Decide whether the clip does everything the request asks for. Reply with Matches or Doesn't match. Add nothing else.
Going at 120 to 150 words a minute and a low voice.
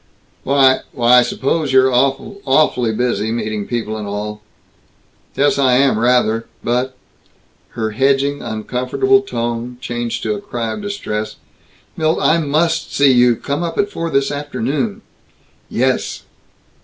Matches